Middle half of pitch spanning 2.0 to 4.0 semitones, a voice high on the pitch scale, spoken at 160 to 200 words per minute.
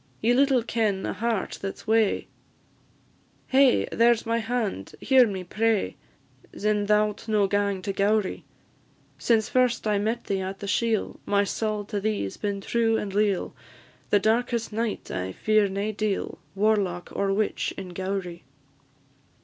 Yes: narrow, 2.4 semitones; high, 210 Hz; average, 165 wpm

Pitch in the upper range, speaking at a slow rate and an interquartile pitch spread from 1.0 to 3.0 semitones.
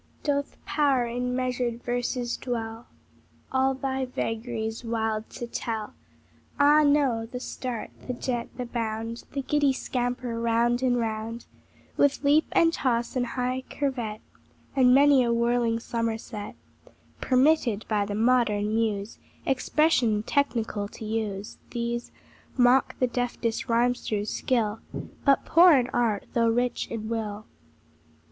Yes: high, 240 Hz; slow, 130 wpm; narrow, 2.4 semitones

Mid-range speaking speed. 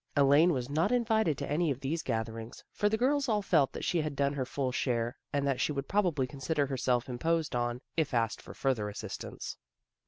No: fast, 220 wpm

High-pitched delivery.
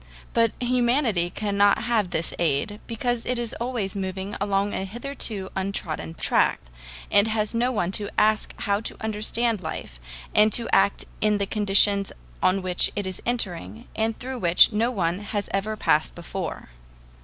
Yes: high, 205 Hz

